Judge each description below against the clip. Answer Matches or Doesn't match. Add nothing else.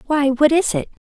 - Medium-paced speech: Doesn't match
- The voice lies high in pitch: Matches